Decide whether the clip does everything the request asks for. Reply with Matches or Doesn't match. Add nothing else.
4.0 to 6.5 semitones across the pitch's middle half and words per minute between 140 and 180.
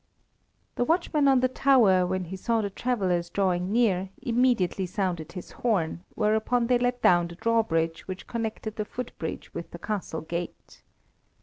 Matches